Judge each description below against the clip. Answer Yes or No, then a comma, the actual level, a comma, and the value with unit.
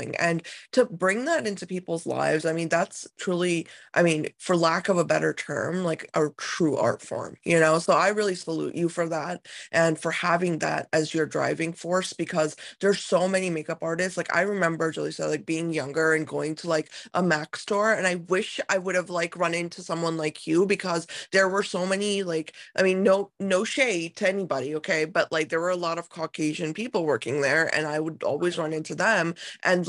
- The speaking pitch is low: No, medium, 170 Hz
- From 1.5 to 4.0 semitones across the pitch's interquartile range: Yes, narrow, 2.5 semitones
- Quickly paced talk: Yes, fast, 215 wpm